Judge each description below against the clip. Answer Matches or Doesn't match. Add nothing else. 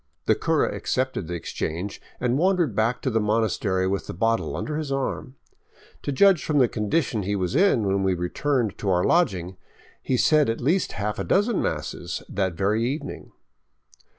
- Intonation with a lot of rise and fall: Matches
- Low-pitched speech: Matches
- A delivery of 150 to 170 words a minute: Doesn't match